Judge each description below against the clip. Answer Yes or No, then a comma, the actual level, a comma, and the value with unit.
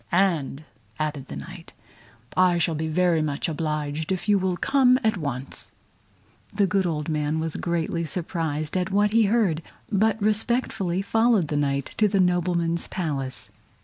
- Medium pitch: Yes, medium, 170 Hz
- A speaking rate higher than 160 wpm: No, average, 155 wpm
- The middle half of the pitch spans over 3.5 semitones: Yes, average, 4.3 semitones